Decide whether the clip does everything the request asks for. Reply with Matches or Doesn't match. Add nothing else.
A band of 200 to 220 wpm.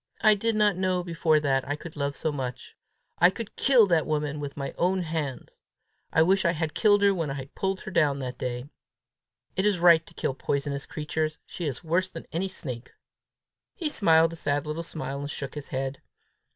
Matches